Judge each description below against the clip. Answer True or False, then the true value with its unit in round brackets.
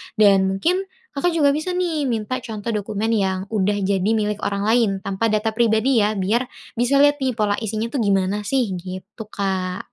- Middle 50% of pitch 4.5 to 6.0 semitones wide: False (4.1 semitones)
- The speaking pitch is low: False (215 Hz)